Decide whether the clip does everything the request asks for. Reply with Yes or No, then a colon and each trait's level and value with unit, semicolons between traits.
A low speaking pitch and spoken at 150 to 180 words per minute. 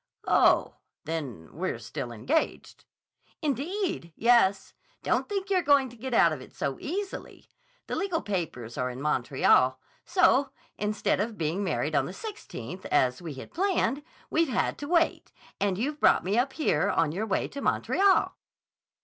No: high, 220 Hz; average, 160 wpm